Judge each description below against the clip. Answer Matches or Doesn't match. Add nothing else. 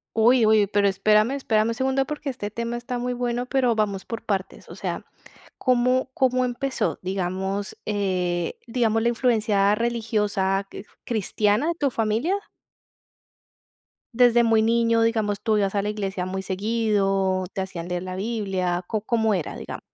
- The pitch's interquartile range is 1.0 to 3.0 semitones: Doesn't match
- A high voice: Matches